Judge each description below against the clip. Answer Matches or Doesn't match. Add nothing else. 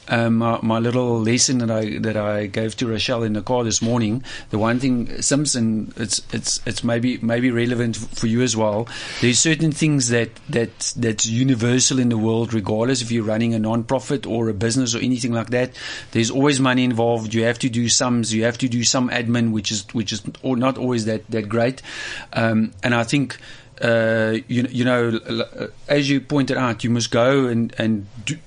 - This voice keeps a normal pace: Doesn't match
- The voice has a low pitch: Matches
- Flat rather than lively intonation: Matches